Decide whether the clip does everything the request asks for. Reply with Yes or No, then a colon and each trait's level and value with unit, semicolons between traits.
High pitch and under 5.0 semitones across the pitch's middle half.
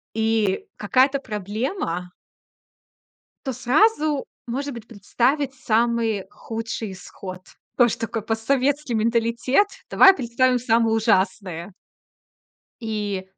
Yes: high, 230 Hz; average, 3.6 semitones